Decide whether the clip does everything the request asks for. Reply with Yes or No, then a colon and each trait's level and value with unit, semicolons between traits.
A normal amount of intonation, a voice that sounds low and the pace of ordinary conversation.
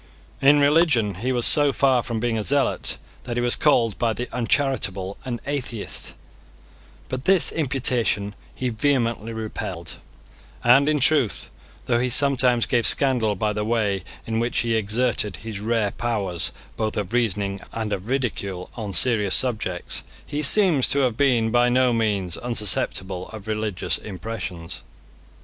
Yes: average, 3.5 semitones; low, 115 Hz; average, 150 wpm